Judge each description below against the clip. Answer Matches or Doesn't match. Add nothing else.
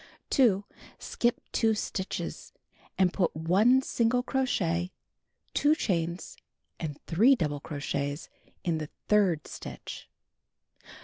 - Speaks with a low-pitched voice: Doesn't match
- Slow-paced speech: Matches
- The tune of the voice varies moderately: Doesn't match